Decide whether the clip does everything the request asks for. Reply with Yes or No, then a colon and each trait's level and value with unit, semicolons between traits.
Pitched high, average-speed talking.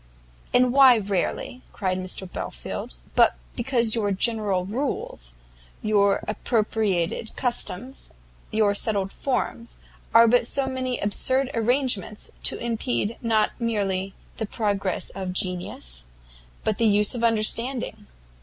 No: high, 215 Hz; slow, 115 wpm